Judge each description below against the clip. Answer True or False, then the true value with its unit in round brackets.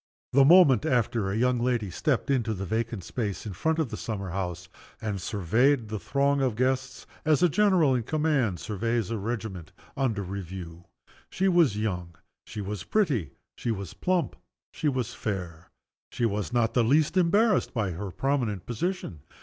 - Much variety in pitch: True (6.0 semitones)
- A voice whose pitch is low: True (115 Hz)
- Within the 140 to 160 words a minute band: False (170 wpm)